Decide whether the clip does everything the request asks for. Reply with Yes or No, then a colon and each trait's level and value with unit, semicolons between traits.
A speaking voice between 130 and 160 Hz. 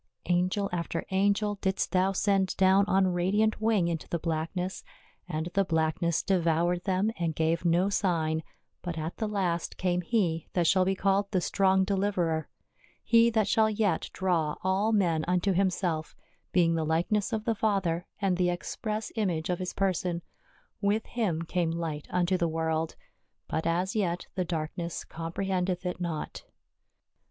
No: medium, 180 Hz